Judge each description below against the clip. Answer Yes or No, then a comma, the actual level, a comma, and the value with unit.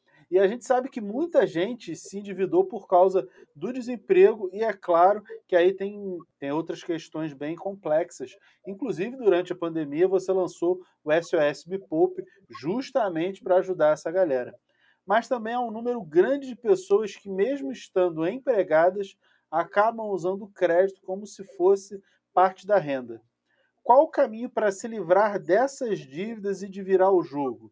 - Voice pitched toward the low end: No, high, 190 Hz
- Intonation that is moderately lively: Yes, average, 4.1 semitones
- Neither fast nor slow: Yes, average, 160 wpm